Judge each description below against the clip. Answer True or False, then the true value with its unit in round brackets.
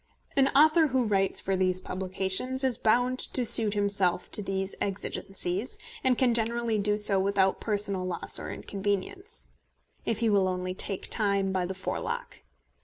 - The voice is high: True (200 Hz)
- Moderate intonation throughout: True (3.7 semitones)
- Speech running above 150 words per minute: True (160 wpm)